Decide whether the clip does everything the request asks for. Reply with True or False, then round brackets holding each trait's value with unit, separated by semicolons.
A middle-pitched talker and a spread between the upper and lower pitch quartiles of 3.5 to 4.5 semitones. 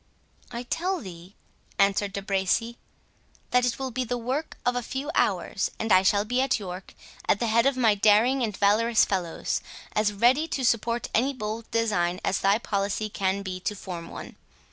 False (215 Hz; 3.8 semitones)